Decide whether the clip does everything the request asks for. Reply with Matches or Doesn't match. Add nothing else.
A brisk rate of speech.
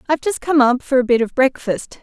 Matches